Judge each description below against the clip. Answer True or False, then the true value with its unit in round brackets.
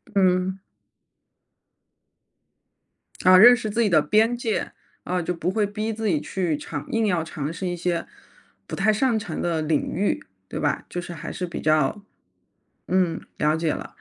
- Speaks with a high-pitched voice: False (180 Hz)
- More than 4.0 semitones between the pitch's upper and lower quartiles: True (4.4 semitones)